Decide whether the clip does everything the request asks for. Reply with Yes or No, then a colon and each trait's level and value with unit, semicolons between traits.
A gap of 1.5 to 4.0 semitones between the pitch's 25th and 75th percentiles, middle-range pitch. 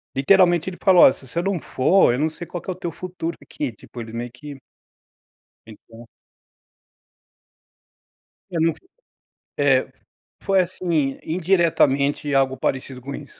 No: average, 4.9 semitones; medium, 150 Hz